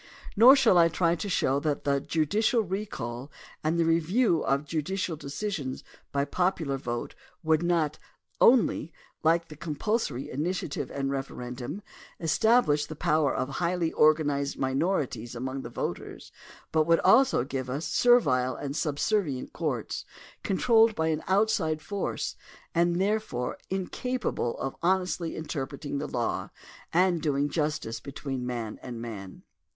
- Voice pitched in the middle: Yes, medium, 155 Hz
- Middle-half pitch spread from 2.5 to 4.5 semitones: No, average, 4.9 semitones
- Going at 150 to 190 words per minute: No, average, 140 wpm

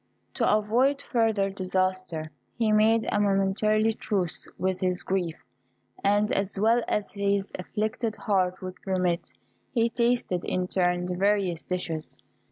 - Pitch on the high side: Yes, high, 195 Hz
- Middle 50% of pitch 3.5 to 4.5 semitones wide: No, average, 2.8 semitones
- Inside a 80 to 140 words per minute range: Yes, slow, 135 wpm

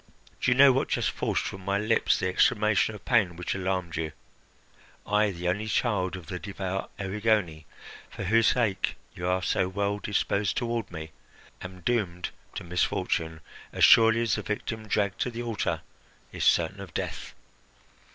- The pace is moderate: Yes, average, 170 wpm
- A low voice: Yes, low, 100 Hz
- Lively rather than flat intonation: No, average, 3.1 semitones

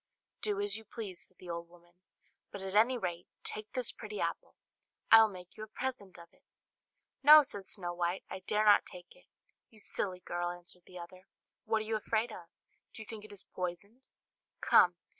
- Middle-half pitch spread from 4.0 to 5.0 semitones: No, average, 3.5 semitones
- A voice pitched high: Yes, high, 200 Hz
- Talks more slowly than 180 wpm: No, average, 200 wpm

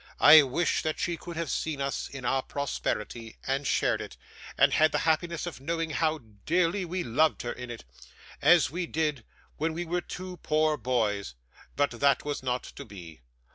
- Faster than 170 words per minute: Yes, average, 185 wpm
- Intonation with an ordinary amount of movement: Yes, average, 4.4 semitones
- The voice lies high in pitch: No, medium, 150 Hz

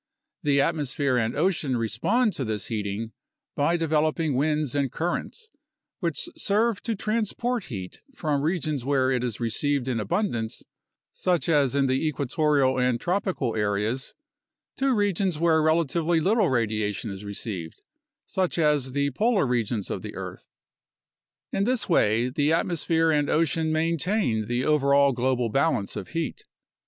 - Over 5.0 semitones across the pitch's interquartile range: Yes, wide, 5.4 semitones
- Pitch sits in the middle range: Yes, medium, 145 Hz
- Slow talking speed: No, average, 145 wpm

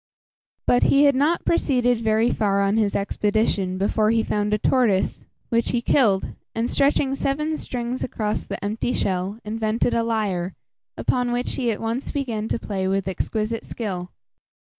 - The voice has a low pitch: No, high, 225 Hz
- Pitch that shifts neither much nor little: Yes, average, 3.3 semitones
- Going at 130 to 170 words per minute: Yes, average, 160 wpm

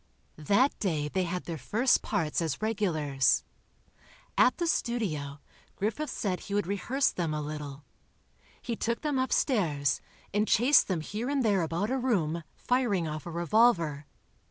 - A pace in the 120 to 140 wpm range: No, average, 155 wpm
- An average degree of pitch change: No, wide, 7.2 semitones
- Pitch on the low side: No, high, 190 Hz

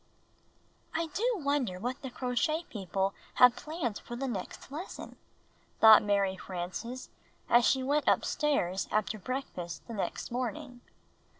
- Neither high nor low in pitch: No, high, 245 Hz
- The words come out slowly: Yes, slow, 125 wpm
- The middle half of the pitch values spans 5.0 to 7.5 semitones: Yes, wide, 5.6 semitones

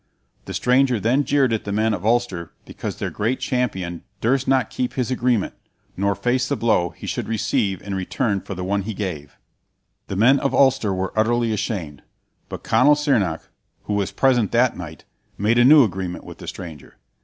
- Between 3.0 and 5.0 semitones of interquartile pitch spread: Yes, average, 4.7 semitones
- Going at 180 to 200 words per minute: Yes, average, 190 wpm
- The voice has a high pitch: No, low, 110 Hz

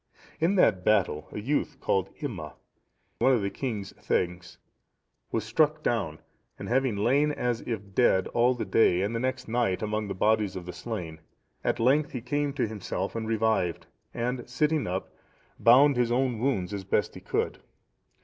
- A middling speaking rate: Yes, average, 180 wpm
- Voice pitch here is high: No, low, 115 Hz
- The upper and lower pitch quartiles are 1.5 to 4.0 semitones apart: No, average, 4.7 semitones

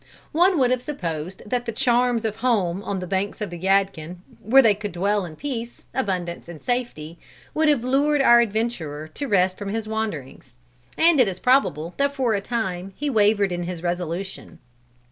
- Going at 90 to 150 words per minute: No, average, 185 wpm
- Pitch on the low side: No, high, 210 Hz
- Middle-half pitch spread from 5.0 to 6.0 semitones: Yes, wide, 5.6 semitones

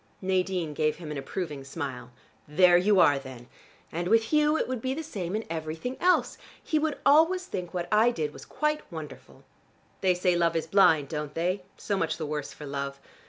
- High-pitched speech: No, medium, 175 Hz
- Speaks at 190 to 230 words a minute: Yes, average, 200 wpm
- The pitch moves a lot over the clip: Yes, wide, 6.3 semitones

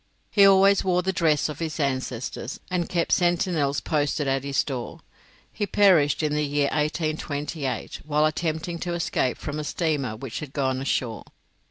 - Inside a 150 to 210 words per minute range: Yes, average, 165 wpm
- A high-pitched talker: No, medium, 150 Hz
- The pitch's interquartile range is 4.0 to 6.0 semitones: No, average, 3.6 semitones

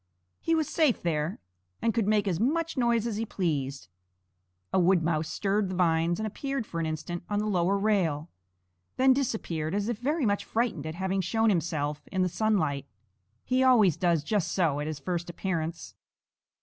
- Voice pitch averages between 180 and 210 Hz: Yes, high, 190 Hz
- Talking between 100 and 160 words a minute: No, average, 185 wpm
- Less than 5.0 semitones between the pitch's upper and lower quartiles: No, average, 5.3 semitones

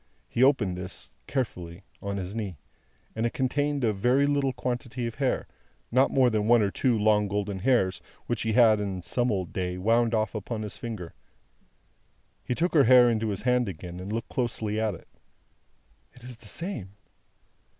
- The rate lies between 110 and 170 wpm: No, average, 180 wpm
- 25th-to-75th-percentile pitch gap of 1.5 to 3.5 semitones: No, average, 3.9 semitones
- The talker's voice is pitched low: Yes, low, 110 Hz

